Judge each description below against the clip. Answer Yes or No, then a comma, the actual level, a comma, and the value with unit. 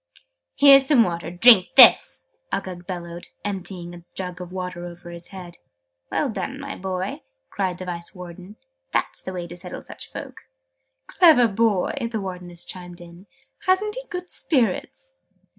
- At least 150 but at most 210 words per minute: Yes, average, 155 wpm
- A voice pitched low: No, medium, 185 Hz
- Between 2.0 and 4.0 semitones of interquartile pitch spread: No, average, 4.8 semitones